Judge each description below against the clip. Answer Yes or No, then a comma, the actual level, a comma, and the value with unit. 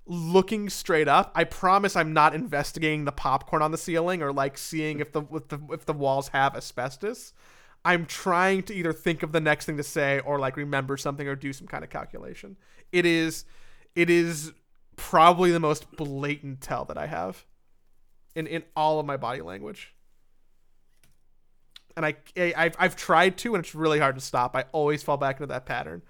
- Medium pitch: Yes, medium, 155 Hz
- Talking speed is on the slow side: No, average, 195 wpm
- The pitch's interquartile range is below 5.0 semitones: Yes, average, 3.1 semitones